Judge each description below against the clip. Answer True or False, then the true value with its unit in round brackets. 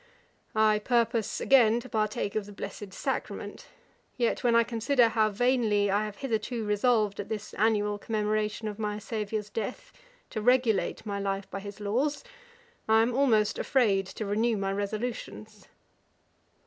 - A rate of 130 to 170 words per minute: True (150 wpm)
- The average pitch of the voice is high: True (215 Hz)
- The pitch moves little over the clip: True (2.1 semitones)